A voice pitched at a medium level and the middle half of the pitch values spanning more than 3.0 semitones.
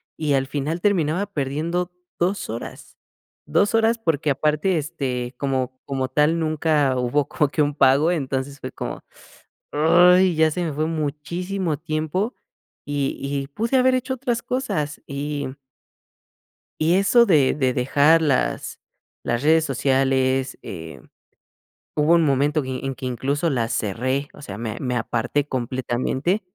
Yes: medium, 145 Hz; average, 4.1 semitones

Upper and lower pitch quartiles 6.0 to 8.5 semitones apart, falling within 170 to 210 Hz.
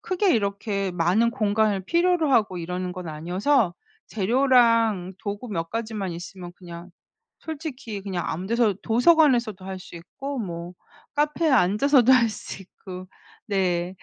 No: average, 5.3 semitones; high, 205 Hz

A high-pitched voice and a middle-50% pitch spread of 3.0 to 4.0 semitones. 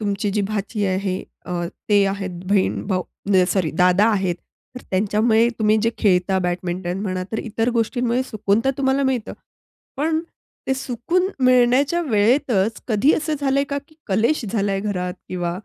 No: high, 210 Hz; average, 4.8 semitones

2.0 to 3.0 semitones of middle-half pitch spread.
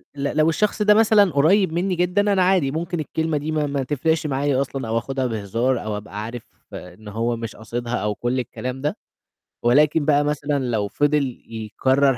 No: average, 5.1 semitones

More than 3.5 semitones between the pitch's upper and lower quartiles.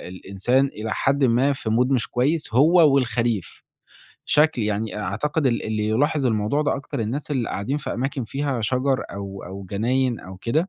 Yes: average, 4.4 semitones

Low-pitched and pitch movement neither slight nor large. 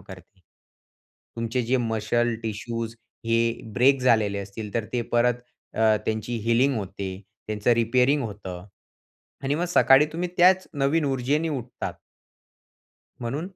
Yes: low, 115 Hz; average, 3.7 semitones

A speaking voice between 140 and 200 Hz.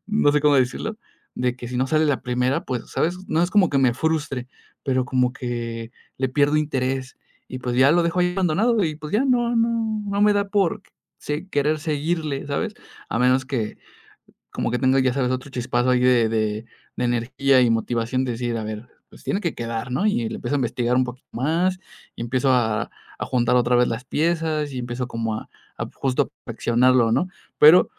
No: low, 130 Hz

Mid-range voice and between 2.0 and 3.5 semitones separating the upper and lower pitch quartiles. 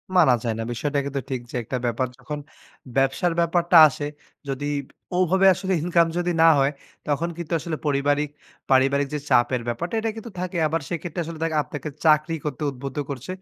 No: medium, 150 Hz; average, 4.0 semitones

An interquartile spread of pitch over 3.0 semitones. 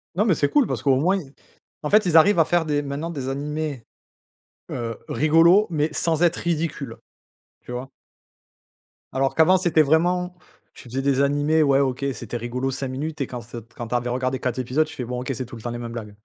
Yes: average, 4.2 semitones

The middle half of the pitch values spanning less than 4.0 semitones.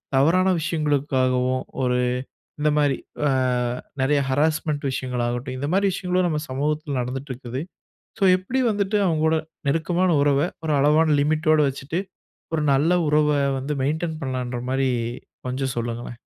Yes: average, 3.4 semitones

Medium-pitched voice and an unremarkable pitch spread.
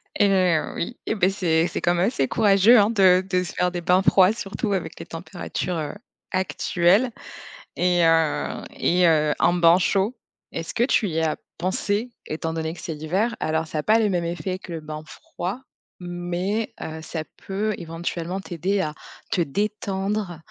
Yes: medium, 180 Hz; average, 3.2 semitones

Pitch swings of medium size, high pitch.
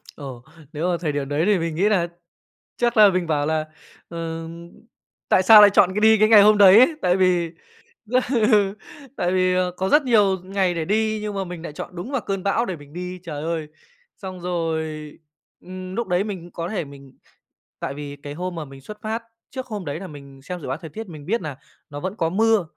No: average, 4.4 semitones; medium, 180 Hz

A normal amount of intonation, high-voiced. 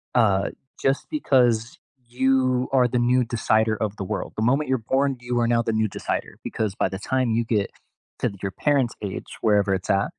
No: average, 3.4 semitones; low, 115 Hz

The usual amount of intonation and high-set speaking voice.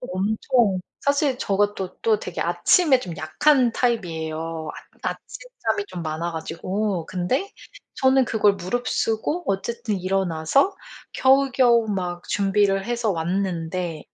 No: wide, 6.0 semitones; high, 200 Hz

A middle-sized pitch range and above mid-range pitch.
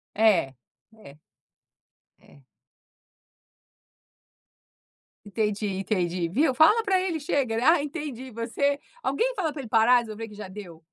No: wide, 6.0 semitones; high, 230 Hz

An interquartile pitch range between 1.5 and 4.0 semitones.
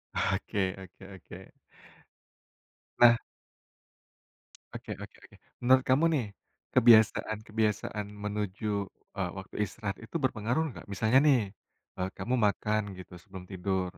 Yes: average, 3.3 semitones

